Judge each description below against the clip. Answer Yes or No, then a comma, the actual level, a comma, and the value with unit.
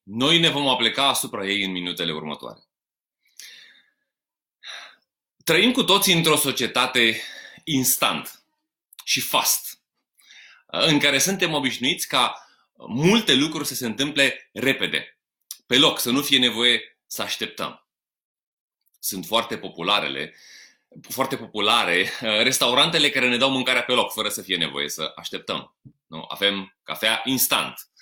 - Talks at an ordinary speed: Yes, average, 125 wpm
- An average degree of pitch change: Yes, average, 4.9 semitones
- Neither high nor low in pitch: No, low, 130 Hz